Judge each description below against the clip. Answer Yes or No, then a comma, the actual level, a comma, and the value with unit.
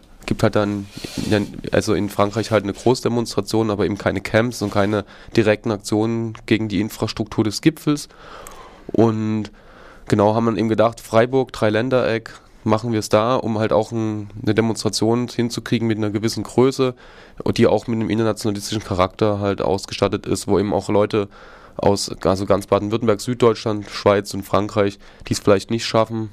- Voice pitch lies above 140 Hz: No, low, 110 Hz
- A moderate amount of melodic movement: No, narrow, 1.7 semitones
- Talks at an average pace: Yes, average, 160 wpm